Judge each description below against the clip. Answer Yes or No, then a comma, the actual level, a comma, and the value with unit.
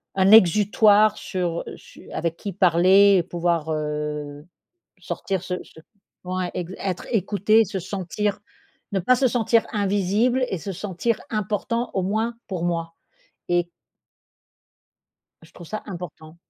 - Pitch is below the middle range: No, high, 190 Hz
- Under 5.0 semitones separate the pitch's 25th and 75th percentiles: Yes, average, 3.4 semitones